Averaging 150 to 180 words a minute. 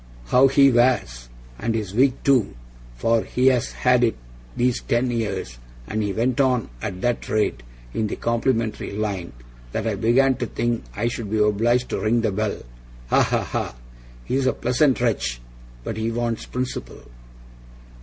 Yes: average, 165 wpm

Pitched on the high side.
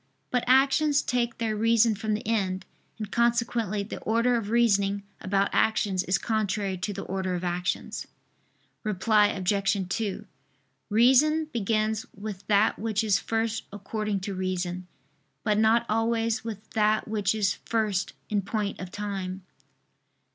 Yes: high, 215 Hz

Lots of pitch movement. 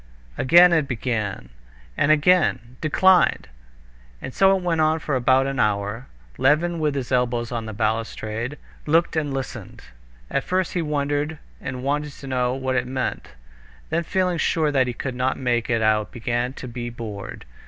No: average, 4.4 semitones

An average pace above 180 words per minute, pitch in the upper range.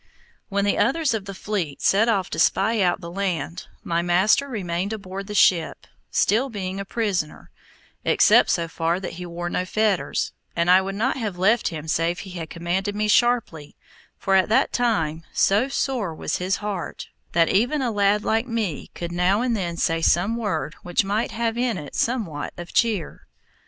Yes: average, 190 wpm; high, 195 Hz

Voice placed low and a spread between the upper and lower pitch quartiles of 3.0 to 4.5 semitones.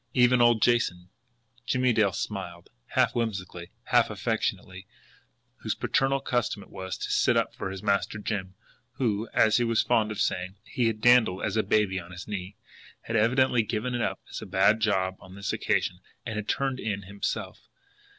Yes: low, 105 Hz; average, 3.9 semitones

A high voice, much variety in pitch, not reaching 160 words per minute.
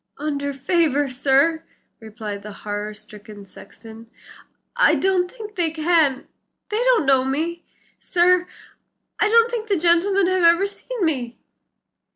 Yes: very high, 320 Hz; wide, 6.5 semitones; slow, 135 wpm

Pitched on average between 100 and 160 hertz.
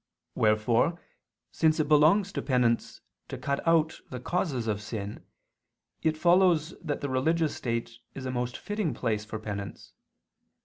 Yes: low, 135 Hz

